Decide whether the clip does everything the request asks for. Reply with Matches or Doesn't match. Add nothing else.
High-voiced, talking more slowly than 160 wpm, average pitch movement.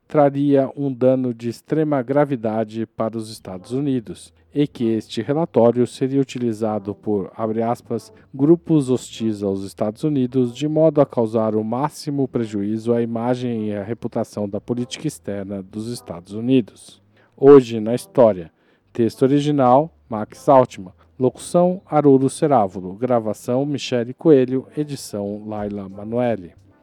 Doesn't match